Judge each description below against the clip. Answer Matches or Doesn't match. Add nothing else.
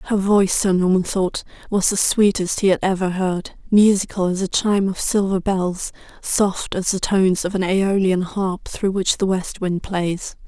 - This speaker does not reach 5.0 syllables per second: Matches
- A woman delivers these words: Matches